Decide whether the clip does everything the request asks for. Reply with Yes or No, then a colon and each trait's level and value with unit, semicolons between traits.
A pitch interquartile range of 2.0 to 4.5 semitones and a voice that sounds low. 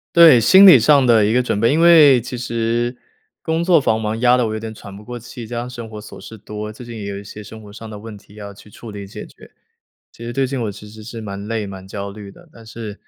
Yes: average, 2.7 semitones; low, 115 Hz